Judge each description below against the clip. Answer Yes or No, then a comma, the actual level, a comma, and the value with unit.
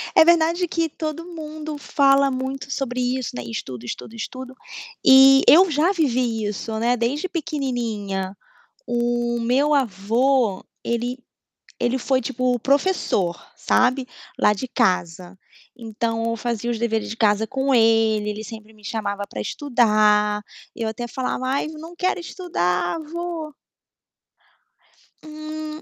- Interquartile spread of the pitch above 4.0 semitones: Yes, average, 4.8 semitones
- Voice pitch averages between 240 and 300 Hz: Yes, high, 245 Hz